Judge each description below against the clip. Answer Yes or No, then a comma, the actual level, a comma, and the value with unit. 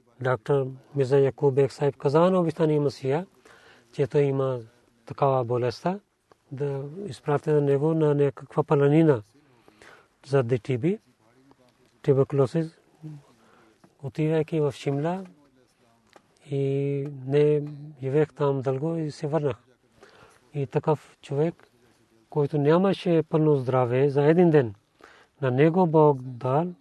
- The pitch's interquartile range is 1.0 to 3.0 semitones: Yes, narrow, 2.6 semitones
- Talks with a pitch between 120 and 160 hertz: Yes, medium, 140 Hz